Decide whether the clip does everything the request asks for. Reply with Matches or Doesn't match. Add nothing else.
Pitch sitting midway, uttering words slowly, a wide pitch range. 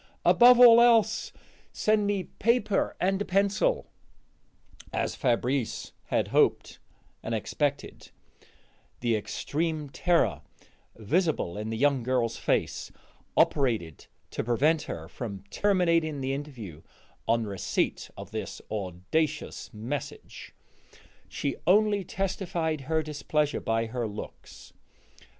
Matches